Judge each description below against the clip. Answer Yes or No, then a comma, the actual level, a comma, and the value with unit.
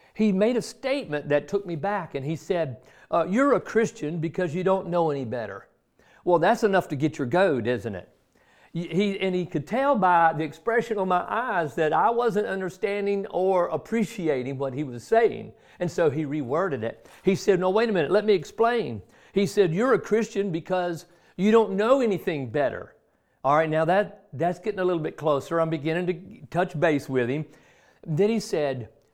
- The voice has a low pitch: No, medium, 175 Hz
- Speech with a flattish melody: No, average, 4.9 semitones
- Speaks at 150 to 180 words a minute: No, average, 200 wpm